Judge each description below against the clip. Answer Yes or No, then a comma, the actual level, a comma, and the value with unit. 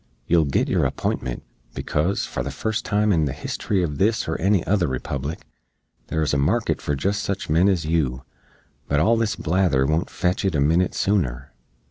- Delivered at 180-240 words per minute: Yes, average, 185 wpm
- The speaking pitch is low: Yes, very low, 80 Hz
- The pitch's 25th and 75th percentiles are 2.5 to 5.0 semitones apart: No, wide, 5.5 semitones